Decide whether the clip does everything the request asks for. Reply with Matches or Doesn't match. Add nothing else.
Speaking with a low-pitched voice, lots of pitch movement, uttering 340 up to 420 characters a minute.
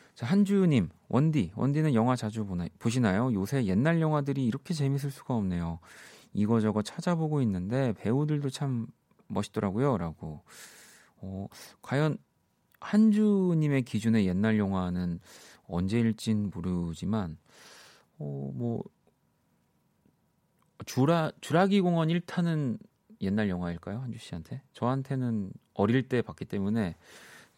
Doesn't match